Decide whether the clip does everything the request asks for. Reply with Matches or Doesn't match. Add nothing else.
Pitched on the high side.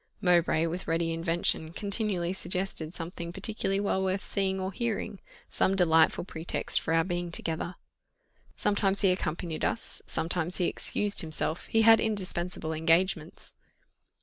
Doesn't match